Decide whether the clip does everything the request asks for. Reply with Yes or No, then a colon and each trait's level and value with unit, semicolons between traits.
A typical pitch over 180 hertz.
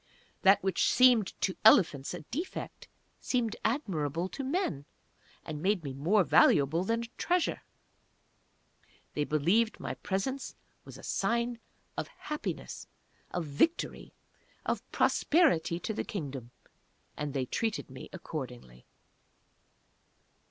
Yes: high, 190 Hz